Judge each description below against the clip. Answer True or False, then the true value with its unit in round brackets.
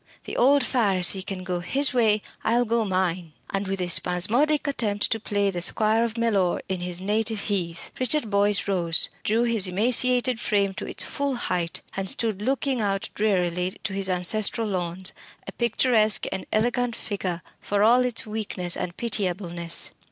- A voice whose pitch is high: True (205 Hz)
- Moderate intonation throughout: True (4.0 semitones)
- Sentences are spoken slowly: False (165 wpm)